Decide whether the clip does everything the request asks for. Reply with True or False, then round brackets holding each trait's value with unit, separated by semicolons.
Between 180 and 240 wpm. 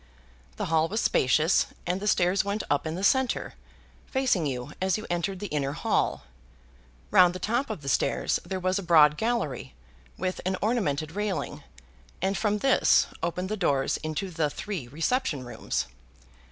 False (165 wpm)